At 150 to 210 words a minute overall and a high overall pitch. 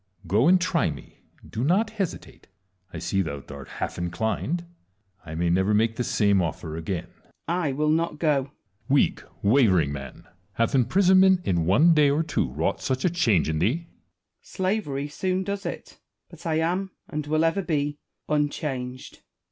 No: average, 175 wpm; medium, 140 Hz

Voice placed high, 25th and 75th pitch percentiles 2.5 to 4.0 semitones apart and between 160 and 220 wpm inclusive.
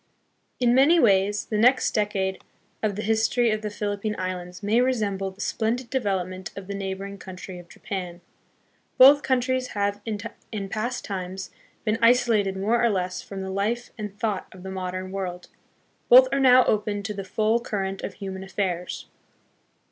Yes: high, 205 Hz; average, 3.2 semitones; average, 170 wpm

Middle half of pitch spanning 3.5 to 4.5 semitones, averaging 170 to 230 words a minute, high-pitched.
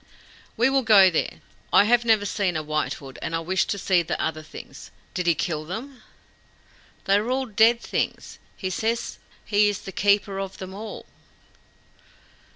Yes: average, 4.0 semitones; average, 175 wpm; high, 200 Hz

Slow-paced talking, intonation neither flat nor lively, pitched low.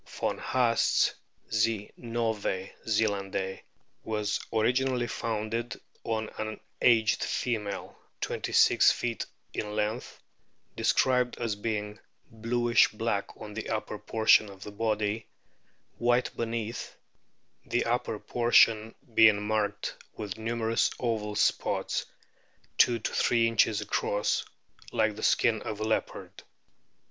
No: slow, 115 wpm; narrow, 1.8 semitones; low, 110 Hz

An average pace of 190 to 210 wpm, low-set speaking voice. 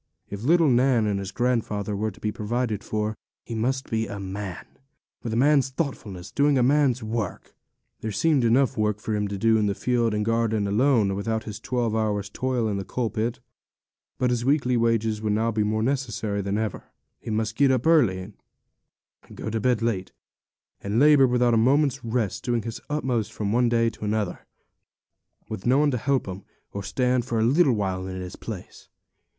Yes: average, 195 wpm; low, 115 Hz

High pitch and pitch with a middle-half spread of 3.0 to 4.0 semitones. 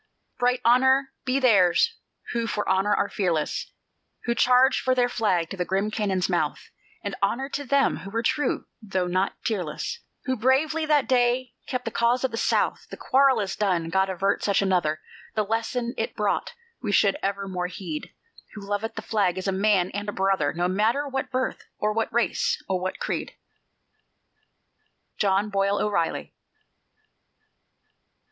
No: high, 210 Hz; average, 4.7 semitones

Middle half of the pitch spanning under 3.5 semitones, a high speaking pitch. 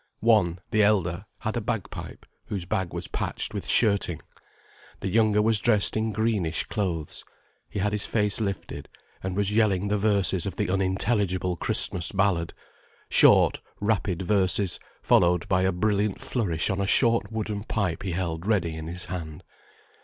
No: average, 2.8 semitones; low, 100 Hz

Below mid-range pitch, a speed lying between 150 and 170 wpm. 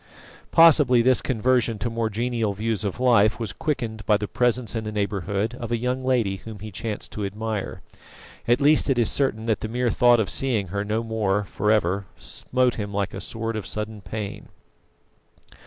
No: low, 110 Hz; average, 190 wpm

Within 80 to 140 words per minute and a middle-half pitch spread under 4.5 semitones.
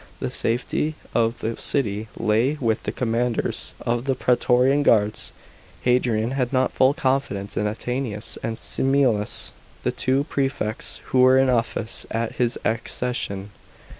Yes: slow, 135 wpm; average, 2.8 semitones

